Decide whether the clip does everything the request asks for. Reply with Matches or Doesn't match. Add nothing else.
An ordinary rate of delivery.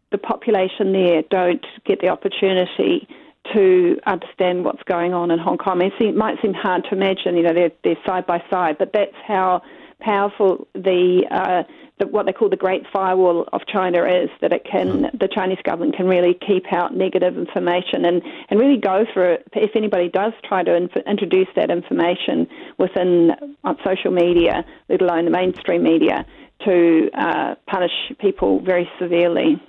Matches